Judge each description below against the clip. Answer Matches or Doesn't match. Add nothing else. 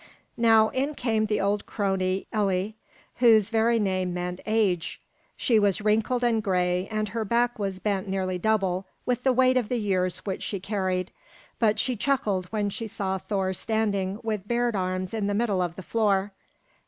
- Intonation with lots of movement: Doesn't match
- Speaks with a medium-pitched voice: Doesn't match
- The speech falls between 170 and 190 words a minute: Matches